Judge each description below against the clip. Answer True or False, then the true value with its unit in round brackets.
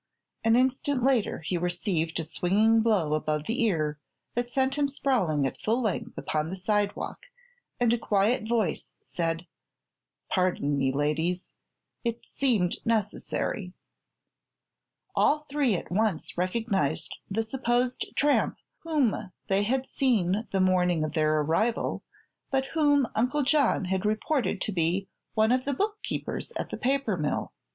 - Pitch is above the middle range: True (215 Hz)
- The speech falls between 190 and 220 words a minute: False (140 wpm)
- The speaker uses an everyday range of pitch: False (6.3 semitones)